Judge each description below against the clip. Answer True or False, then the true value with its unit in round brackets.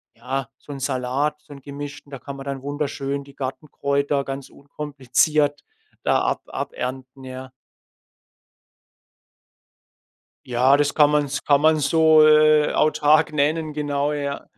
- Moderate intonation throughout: False (1.7 semitones)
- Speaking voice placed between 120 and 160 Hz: True (140 Hz)